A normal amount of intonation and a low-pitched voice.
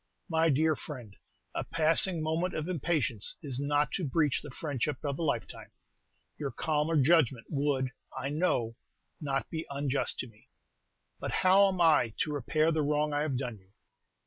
No: average, 3.3 semitones; medium, 150 Hz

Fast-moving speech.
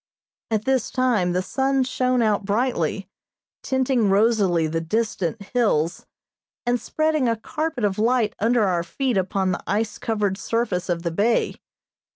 No: average, 150 wpm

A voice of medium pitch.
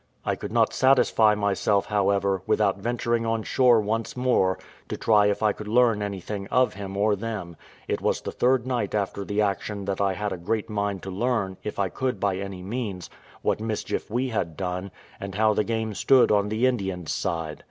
No: low, 105 Hz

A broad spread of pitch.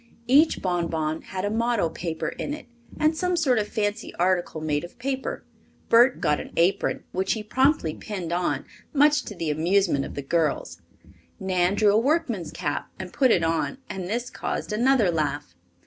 Yes: wide, 6.5 semitones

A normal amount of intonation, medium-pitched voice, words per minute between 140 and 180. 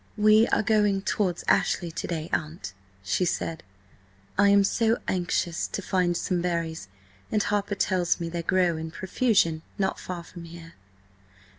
Yes: average, 3.1 semitones; medium, 180 Hz; average, 155 wpm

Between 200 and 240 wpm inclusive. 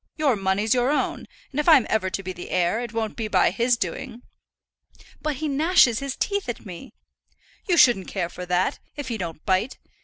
Yes: fast, 205 wpm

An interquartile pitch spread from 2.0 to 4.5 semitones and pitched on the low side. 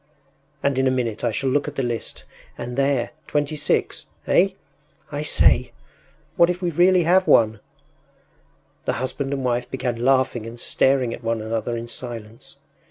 Yes: average, 3.5 semitones; low, 130 Hz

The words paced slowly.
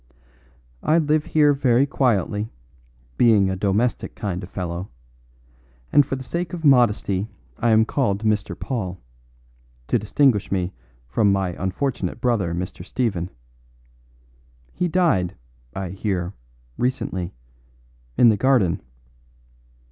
Yes: slow, 120 wpm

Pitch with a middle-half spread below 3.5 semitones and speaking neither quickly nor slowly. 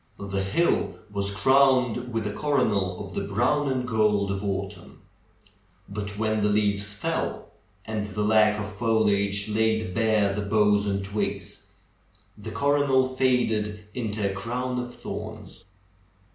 Yes: average, 2.7 semitones; average, 145 wpm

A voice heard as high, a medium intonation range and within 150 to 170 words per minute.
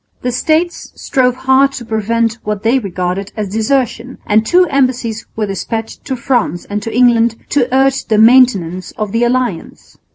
Yes: high, 230 Hz; average, 3.4 semitones; average, 165 wpm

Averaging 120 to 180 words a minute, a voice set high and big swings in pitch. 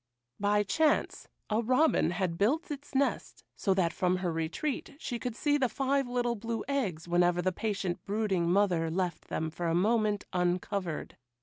Yes: average, 170 wpm; high, 200 Hz; wide, 5.7 semitones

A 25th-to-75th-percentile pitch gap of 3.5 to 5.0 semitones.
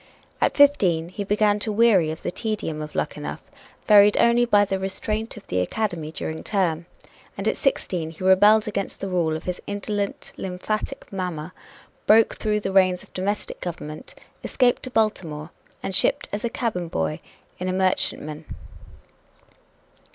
Yes: average, 3.9 semitones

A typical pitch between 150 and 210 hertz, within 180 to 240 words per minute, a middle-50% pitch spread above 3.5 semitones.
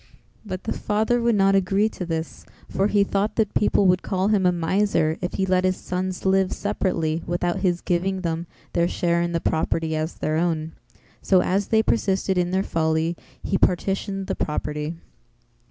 No: medium, 185 Hz; average, 185 wpm; narrow, 2.5 semitones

